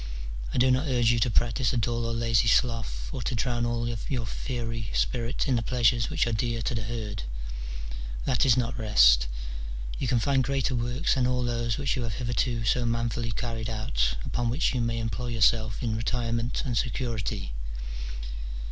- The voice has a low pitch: Yes, low, 115 Hz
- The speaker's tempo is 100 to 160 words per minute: No, average, 185 wpm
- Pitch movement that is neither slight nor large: No, narrow, 1.6 semitones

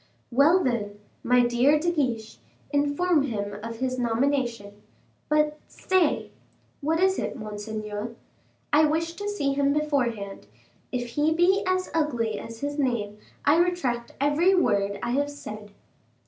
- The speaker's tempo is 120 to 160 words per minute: Yes, average, 145 wpm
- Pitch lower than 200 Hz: No, very high, 275 Hz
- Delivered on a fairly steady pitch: No, average, 5.2 semitones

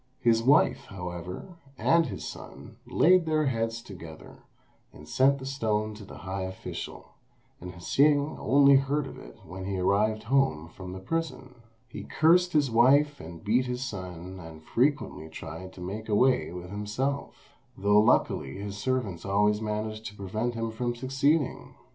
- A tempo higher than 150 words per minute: Yes, average, 160 wpm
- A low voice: Yes, low, 110 Hz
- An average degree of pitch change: No, wide, 6.2 semitones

